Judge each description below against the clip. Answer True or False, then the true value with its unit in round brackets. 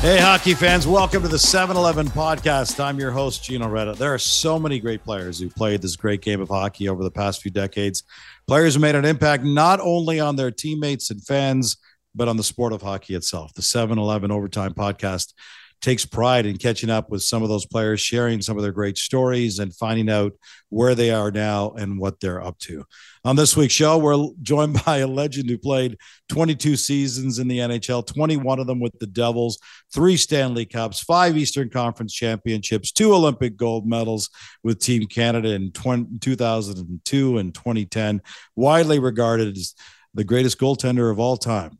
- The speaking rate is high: False (190 wpm)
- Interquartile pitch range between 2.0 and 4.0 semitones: False (4.8 semitones)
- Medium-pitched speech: False (120 Hz)